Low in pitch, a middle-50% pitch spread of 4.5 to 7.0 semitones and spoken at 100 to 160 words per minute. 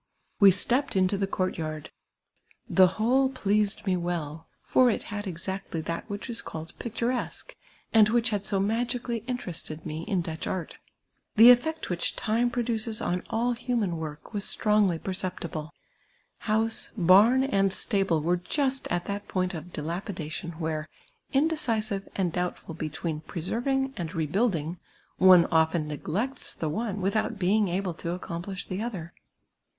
No: high, 195 Hz; average, 5.0 semitones; average, 150 wpm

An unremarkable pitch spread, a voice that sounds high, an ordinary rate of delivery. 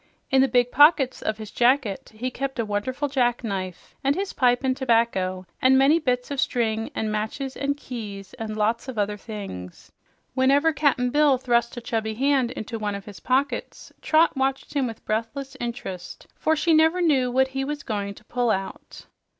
Yes: average, 4.0 semitones; high, 245 Hz; average, 185 wpm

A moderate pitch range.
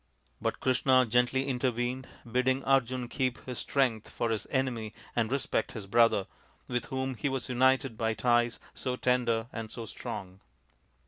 No: narrow, 2.3 semitones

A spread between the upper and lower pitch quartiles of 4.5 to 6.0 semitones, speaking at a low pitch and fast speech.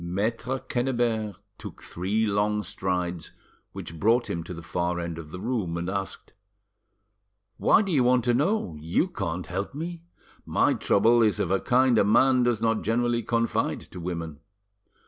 No: wide, 5.4 semitones; low, 105 Hz; average, 165 wpm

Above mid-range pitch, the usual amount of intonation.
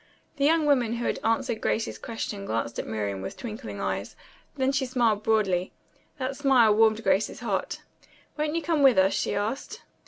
Yes: high, 230 Hz; average, 4.7 semitones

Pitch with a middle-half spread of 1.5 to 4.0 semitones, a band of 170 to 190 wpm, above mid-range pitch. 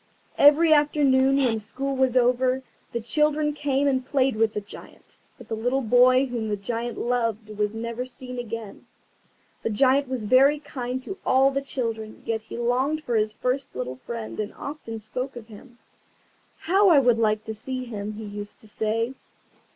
Yes: average, 3.5 semitones; average, 180 wpm; high, 245 Hz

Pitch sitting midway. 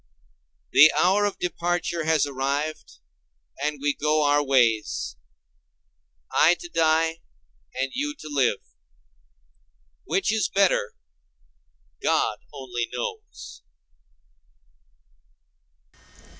Yes: medium, 145 Hz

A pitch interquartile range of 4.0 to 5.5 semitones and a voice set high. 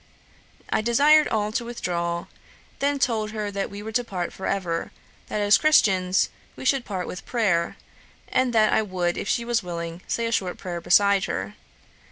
Yes: average, 4.6 semitones; high, 205 Hz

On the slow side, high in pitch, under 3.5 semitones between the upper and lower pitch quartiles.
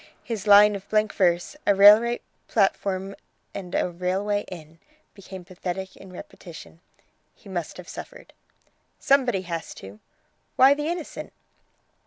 Yes: slow, 130 wpm; high, 195 Hz; average, 2.8 semitones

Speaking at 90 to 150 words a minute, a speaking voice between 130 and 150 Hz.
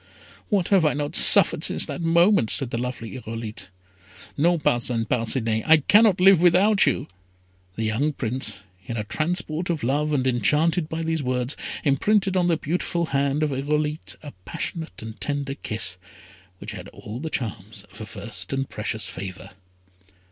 No: average, 165 wpm; medium, 140 Hz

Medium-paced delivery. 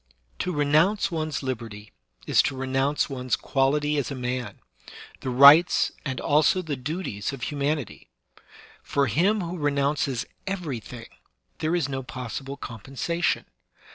No: slow, 130 wpm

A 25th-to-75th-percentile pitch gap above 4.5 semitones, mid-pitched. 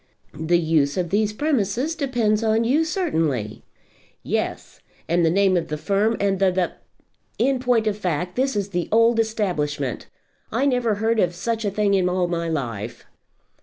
No: average, 5.0 semitones; high, 200 Hz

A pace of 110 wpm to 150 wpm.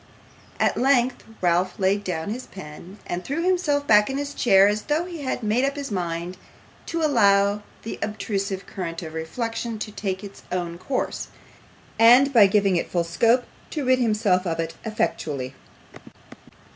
No: average, 165 wpm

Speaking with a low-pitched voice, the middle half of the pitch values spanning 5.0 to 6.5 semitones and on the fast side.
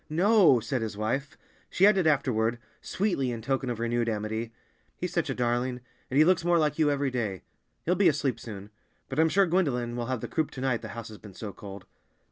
Yes: low, 130 Hz; wide, 5.5 semitones; fast, 220 wpm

